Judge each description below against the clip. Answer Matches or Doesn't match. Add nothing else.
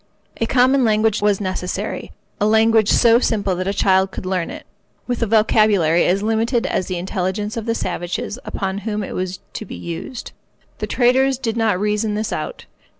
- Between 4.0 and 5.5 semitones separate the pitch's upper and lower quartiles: Doesn't match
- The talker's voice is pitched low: Doesn't match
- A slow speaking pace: Doesn't match